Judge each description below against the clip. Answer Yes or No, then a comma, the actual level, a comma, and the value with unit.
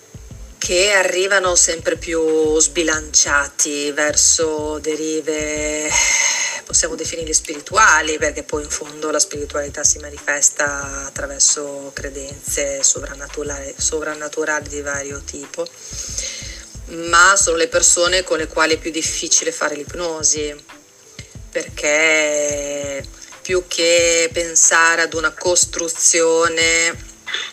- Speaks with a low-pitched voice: No, medium, 155 Hz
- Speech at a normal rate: No, slow, 95 wpm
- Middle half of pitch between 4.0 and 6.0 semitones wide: No, narrow, 2.5 semitones